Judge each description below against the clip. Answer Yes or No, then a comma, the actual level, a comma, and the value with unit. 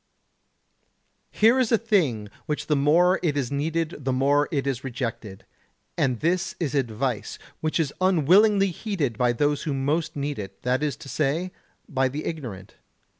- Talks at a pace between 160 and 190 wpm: Yes, average, 165 wpm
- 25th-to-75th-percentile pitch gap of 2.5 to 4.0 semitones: No, average, 4.5 semitones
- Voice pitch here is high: No, medium, 145 Hz